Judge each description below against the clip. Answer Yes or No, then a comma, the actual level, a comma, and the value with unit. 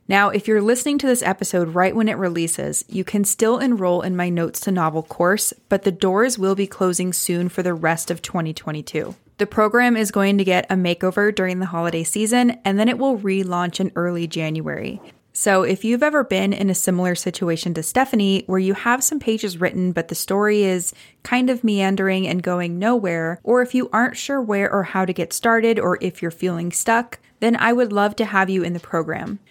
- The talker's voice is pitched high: Yes, high, 195 Hz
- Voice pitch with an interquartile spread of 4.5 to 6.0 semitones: No, average, 3.8 semitones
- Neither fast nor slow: No, fast, 215 wpm